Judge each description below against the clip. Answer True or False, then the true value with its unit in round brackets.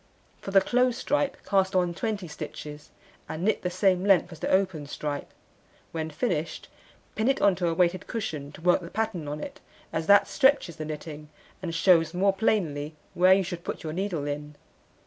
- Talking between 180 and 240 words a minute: True (190 wpm)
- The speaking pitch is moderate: True (180 Hz)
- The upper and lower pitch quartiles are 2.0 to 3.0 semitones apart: False (4.0 semitones)